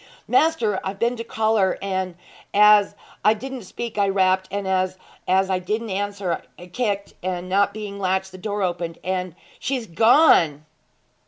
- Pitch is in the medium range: No, high, 195 Hz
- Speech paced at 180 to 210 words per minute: No, average, 160 wpm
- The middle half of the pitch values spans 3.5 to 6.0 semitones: No, narrow, 2.4 semitones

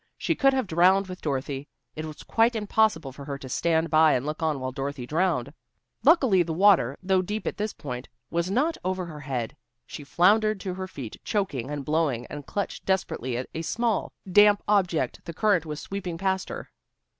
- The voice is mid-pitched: Yes, medium, 170 Hz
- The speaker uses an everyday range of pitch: No, wide, 5.7 semitones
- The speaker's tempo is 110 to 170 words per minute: No, average, 195 wpm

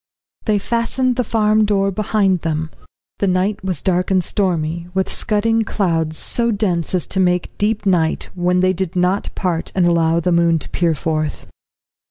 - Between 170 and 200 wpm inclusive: Yes, average, 175 wpm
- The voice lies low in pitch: No, medium, 185 Hz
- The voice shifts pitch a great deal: No, average, 3.4 semitones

